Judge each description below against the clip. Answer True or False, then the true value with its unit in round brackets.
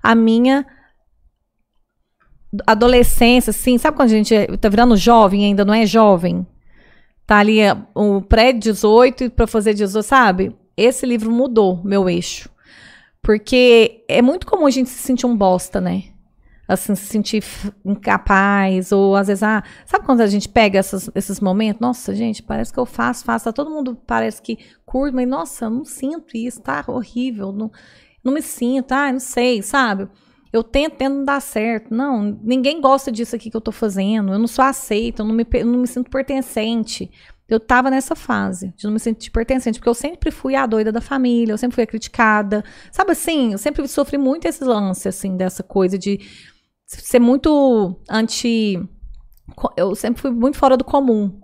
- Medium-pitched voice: False (230 Hz)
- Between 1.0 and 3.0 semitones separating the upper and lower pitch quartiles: False (3.8 semitones)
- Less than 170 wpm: False (180 wpm)